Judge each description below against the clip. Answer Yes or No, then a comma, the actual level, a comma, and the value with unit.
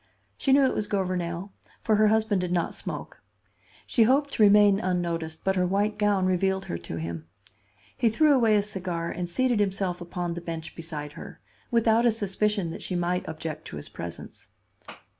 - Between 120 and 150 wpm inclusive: No, average, 185 wpm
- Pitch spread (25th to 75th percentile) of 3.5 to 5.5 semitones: Yes, average, 3.8 semitones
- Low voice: No, high, 190 Hz